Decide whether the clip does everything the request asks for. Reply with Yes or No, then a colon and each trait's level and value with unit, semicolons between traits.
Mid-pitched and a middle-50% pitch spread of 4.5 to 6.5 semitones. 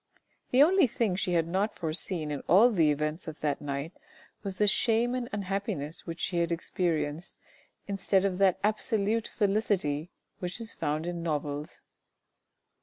Yes: medium, 180 Hz; average, 4.9 semitones